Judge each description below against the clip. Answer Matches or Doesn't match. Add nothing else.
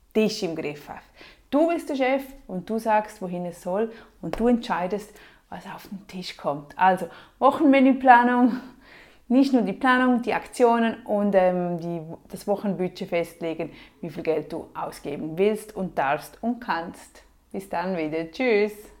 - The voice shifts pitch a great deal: Matches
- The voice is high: Matches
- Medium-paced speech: Matches